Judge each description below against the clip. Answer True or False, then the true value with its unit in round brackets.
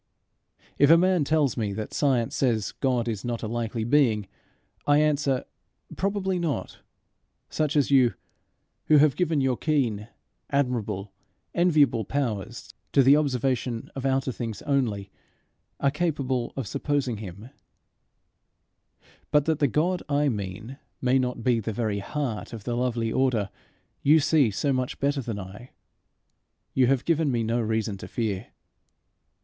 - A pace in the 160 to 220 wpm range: False (145 wpm)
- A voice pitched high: False (130 Hz)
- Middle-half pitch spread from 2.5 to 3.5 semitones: False (4.3 semitones)